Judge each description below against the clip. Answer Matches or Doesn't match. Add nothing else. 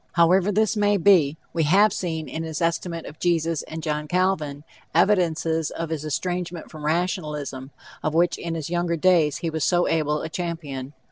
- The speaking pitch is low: Doesn't match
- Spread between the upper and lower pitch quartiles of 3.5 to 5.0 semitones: Doesn't match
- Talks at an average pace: Matches